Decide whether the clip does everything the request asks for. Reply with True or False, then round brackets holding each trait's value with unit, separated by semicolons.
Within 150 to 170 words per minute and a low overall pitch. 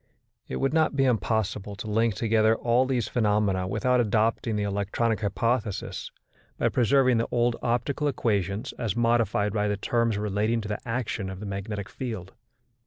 True (165 wpm; 110 Hz)